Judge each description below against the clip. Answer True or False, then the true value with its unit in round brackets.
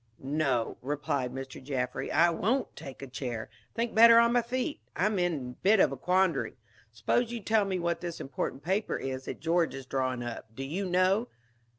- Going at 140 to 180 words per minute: False (195 wpm)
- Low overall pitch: False (165 Hz)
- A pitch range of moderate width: False (7.3 semitones)